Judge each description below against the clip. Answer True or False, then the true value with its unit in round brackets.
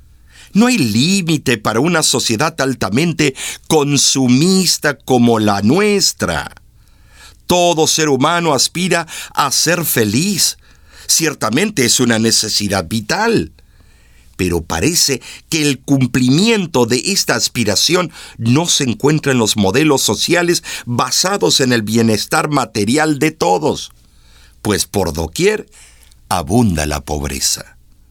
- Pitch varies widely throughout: True (7.0 semitones)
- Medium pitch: False (130 Hz)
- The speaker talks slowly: True (110 wpm)